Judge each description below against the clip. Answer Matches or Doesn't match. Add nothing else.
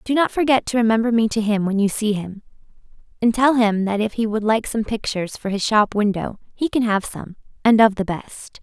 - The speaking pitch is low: Doesn't match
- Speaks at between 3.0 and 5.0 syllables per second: Doesn't match